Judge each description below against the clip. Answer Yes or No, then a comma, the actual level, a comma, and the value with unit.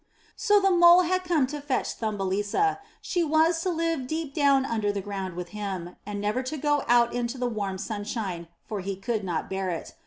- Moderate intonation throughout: No, wide, 7.8 semitones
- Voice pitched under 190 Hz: No, high, 240 Hz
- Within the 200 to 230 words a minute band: Yes, fast, 205 wpm